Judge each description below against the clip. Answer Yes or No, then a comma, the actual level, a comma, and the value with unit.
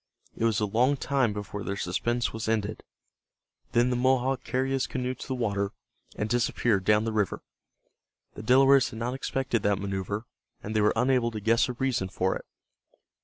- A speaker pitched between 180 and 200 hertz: No, low, 115 Hz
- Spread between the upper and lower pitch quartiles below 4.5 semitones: Yes, average, 3.5 semitones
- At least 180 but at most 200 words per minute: Yes, average, 185 wpm